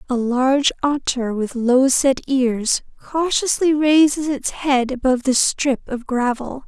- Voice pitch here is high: Yes, very high, 265 Hz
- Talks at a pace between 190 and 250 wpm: No, average, 145 wpm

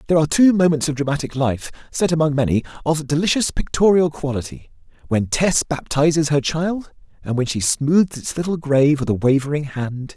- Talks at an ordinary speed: Yes, average, 175 wpm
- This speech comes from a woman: No, male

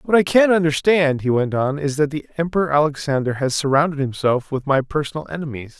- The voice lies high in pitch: No, medium, 150 Hz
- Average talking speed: Yes, average, 195 wpm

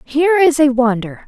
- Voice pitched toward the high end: Yes, very high, 280 Hz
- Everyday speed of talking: Yes, average, 190 wpm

